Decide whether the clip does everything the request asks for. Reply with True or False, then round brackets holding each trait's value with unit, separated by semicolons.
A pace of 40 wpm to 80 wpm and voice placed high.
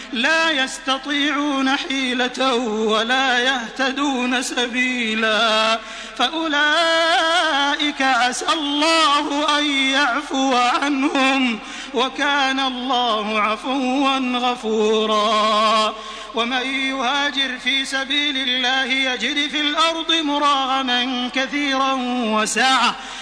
True (70 wpm; 265 Hz)